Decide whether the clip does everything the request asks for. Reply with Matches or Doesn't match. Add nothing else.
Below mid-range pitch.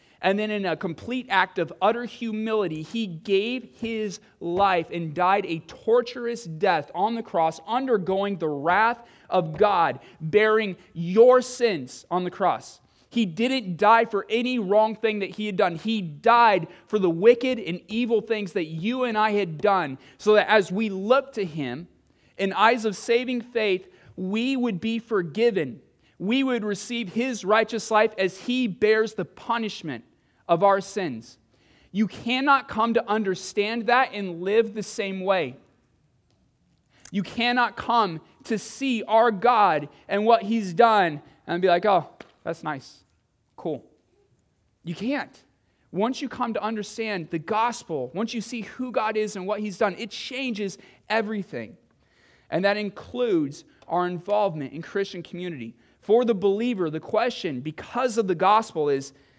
Doesn't match